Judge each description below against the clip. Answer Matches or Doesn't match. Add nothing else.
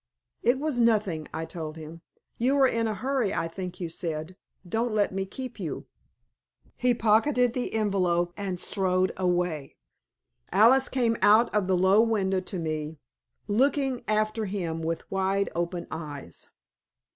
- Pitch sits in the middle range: Doesn't match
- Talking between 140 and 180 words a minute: Matches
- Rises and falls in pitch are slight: Doesn't match